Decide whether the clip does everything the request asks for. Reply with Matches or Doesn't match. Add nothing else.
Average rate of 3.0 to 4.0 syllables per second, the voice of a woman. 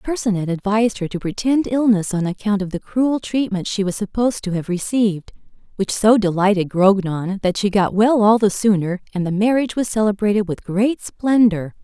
Doesn't match